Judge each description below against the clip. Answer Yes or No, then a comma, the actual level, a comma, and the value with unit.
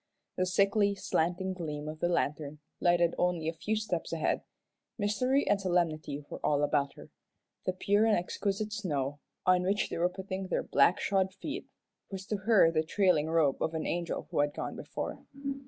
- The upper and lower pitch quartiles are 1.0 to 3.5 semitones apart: No, average, 3.9 semitones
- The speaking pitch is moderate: Yes, medium, 180 Hz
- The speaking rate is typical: Yes, average, 180 wpm